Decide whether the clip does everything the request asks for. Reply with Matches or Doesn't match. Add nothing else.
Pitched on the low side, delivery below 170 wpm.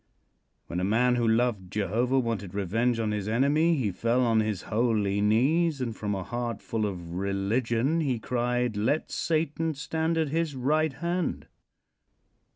Matches